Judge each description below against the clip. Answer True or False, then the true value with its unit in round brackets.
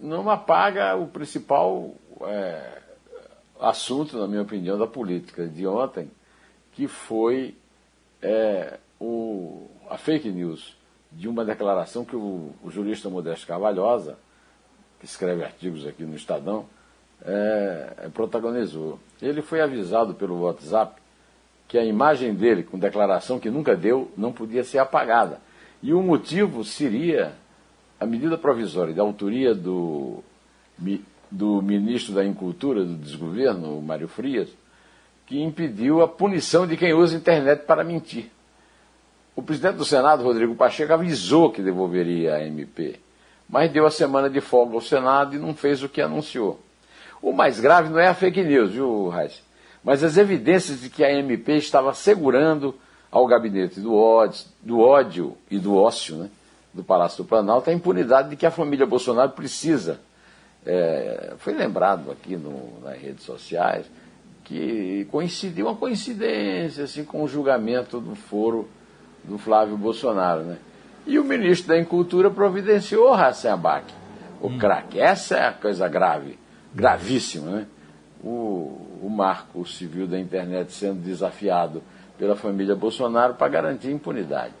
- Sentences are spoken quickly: False (145 wpm)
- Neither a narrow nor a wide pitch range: False (8.0 semitones)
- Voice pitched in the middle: False (120 Hz)